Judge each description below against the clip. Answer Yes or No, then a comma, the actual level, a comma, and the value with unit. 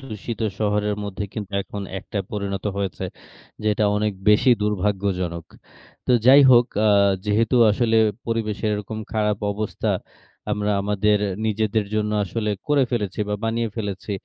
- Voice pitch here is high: No, low, 105 Hz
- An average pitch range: No, narrow, 1.5 semitones